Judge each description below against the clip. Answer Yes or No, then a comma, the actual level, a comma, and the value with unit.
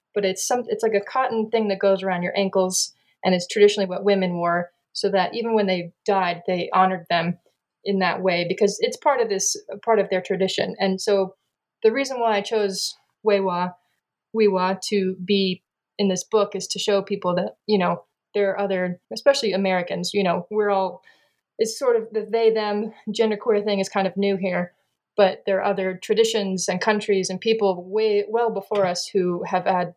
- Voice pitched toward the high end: Yes, high, 195 Hz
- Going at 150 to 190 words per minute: No, average, 200 wpm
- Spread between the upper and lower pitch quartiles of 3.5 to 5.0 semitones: No, narrow, 2.5 semitones